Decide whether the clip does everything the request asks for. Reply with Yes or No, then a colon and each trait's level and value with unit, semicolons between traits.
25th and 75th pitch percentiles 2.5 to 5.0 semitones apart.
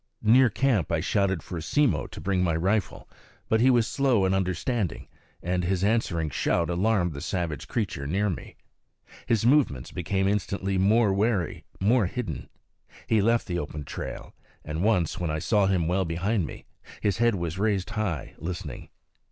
Yes: average, 4.4 semitones